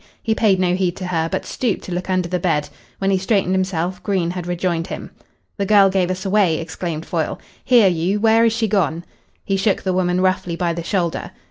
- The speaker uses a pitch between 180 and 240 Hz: Yes, medium, 185 Hz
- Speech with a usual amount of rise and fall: No, narrow, 2.2 semitones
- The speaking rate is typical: No, fast, 220 wpm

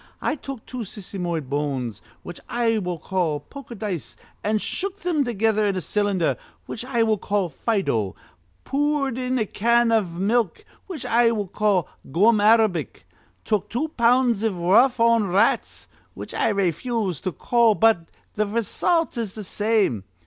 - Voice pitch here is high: Yes, high, 215 Hz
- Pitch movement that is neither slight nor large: Yes, average, 4.3 semitones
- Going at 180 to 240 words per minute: No, average, 155 wpm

